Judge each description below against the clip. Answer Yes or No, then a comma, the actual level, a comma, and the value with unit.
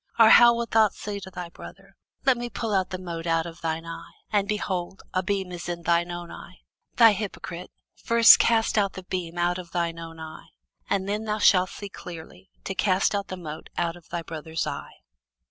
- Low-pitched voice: No, medium, 185 Hz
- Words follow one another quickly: Yes, fast, 215 wpm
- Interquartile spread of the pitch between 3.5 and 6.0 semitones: No, average, 3.1 semitones